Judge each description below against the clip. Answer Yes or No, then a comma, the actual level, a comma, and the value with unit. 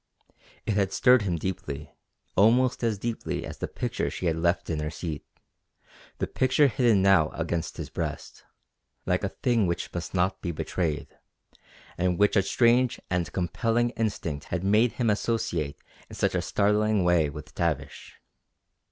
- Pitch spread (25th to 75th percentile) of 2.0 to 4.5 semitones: No, average, 5.2 semitones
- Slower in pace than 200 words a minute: Yes, average, 160 wpm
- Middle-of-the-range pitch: No, very low, 95 Hz